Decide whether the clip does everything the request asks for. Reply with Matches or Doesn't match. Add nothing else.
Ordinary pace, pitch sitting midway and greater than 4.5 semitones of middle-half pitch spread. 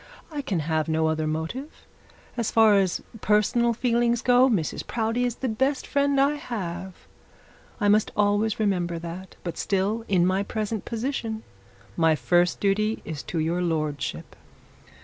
Doesn't match